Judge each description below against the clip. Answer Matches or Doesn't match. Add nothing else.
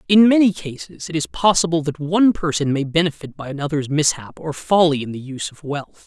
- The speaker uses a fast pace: Matches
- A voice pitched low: Doesn't match